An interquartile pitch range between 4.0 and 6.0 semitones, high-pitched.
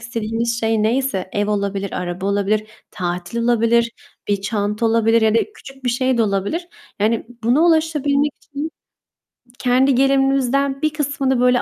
Yes: average, 4.3 semitones; high, 235 Hz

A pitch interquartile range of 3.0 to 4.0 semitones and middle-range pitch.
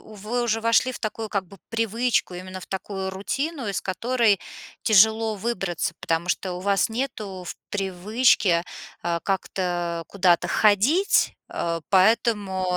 No: average, 3.5 semitones; high, 200 Hz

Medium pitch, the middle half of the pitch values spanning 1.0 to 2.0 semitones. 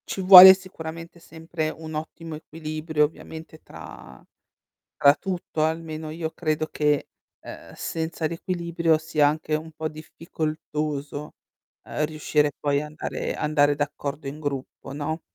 Yes: medium, 155 Hz; narrow, 1.5 semitones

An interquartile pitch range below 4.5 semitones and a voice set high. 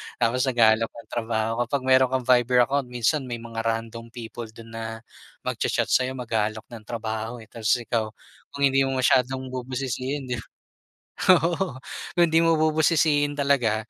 No: average, 2.8 semitones; low, 125 Hz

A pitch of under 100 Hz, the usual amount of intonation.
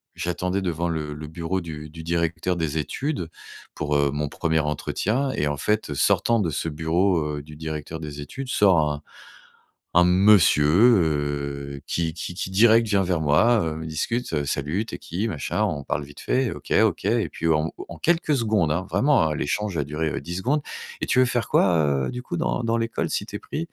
No: very low, 85 Hz; wide, 5.9 semitones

